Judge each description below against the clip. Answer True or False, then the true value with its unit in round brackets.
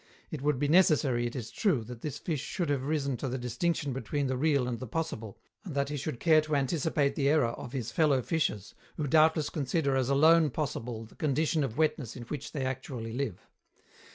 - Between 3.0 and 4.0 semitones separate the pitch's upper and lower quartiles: True (3.7 semitones)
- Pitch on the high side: False (140 Hz)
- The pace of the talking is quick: True (210 wpm)